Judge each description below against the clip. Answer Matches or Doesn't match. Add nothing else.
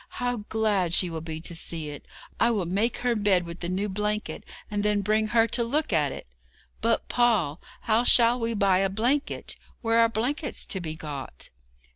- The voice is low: Doesn't match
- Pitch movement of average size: Matches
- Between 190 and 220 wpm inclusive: Matches